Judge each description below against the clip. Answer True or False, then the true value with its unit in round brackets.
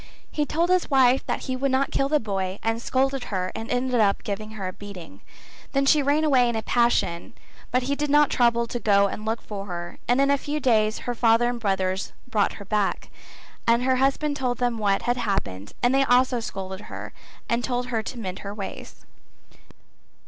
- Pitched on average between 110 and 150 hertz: False (235 Hz)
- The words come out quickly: True (210 wpm)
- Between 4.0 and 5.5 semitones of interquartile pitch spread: True (4.5 semitones)